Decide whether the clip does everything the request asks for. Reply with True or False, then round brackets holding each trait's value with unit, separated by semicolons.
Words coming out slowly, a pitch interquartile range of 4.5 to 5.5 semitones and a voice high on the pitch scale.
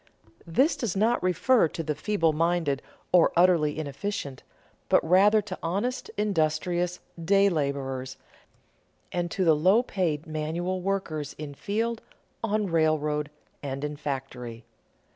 False (130 wpm; 4.8 semitones; 165 Hz)